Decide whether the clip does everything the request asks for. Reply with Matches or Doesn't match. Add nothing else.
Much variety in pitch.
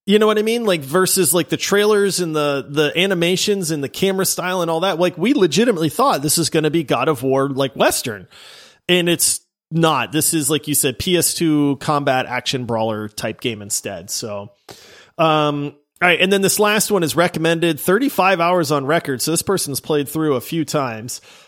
Doesn't match